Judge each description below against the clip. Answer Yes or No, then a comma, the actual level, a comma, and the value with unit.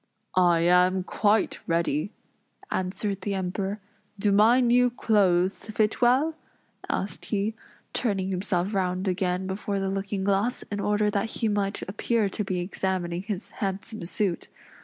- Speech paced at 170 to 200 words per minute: No, average, 140 wpm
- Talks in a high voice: Yes, high, 195 Hz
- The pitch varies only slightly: Yes, narrow, 2.3 semitones